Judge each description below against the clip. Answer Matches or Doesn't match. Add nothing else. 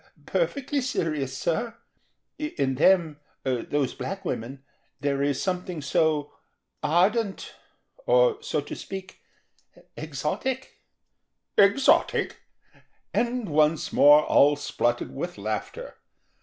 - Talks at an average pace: Doesn't match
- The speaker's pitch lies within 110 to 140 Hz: Doesn't match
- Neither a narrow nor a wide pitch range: Doesn't match